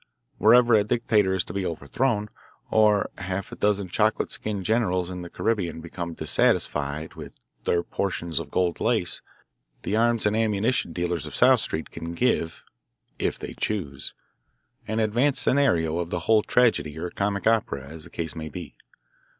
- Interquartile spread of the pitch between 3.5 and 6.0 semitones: Yes, average, 4.5 semitones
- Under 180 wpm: Yes, average, 165 wpm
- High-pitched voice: No, very low, 95 Hz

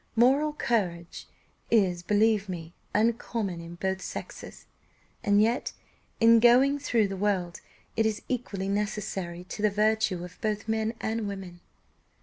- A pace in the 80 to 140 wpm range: Yes, slow, 135 wpm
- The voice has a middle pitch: No, high, 210 Hz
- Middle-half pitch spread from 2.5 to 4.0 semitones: Yes, average, 3.3 semitones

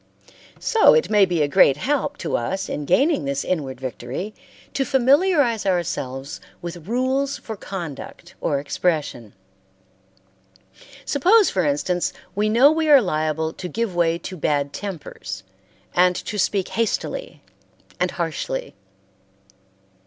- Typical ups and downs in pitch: No, wide, 8.3 semitones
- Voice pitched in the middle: Yes, medium, 180 Hz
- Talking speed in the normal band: No, slow, 130 wpm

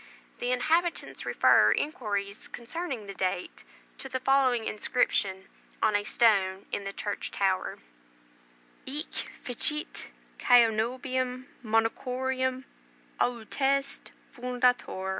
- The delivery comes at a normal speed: No, slow, 95 wpm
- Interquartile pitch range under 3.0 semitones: No, average, 4.0 semitones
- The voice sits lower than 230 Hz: No, high, 245 Hz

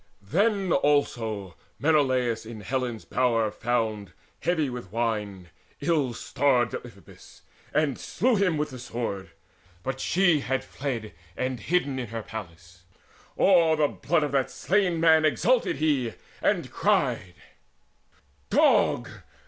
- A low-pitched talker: Yes, low, 130 Hz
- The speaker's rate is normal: No, slow, 125 wpm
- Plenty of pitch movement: Yes, wide, 5.7 semitones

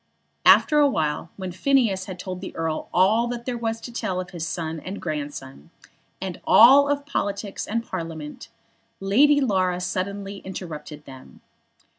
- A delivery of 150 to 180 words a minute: Yes, average, 165 wpm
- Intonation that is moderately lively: No, wide, 5.9 semitones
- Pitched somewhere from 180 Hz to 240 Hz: Yes, high, 190 Hz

